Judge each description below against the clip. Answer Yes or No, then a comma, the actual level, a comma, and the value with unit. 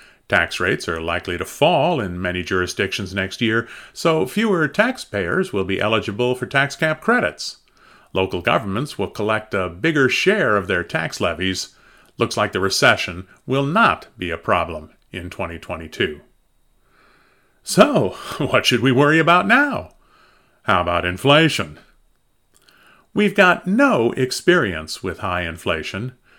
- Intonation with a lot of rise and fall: Yes, wide, 8.7 semitones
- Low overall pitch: Yes, low, 110 Hz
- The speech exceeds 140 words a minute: No, slow, 135 wpm